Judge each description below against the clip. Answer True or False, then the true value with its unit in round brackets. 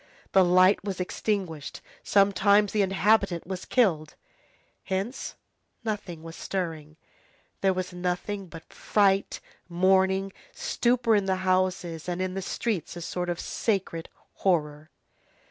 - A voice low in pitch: False (185 Hz)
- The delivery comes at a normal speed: False (125 wpm)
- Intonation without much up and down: True (2.2 semitones)